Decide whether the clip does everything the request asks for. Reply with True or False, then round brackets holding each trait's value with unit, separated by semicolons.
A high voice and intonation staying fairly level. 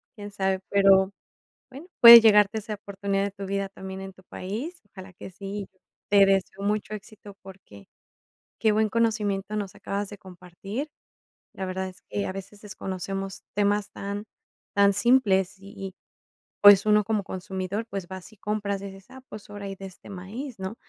True (200 Hz; 1.5 semitones)